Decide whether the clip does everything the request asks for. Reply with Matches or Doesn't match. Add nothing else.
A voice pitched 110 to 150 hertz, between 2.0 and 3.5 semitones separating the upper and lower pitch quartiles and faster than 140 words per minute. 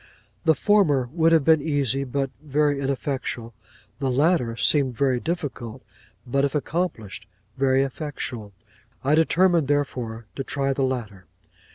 Doesn't match